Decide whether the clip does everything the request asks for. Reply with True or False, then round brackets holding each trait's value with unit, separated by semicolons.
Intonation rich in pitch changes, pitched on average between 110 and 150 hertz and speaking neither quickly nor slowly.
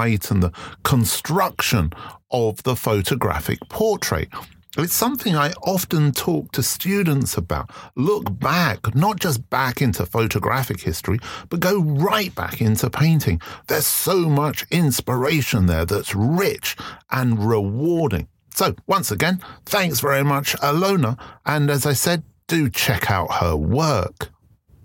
False (6.9 semitones; 135 Hz; 130 wpm)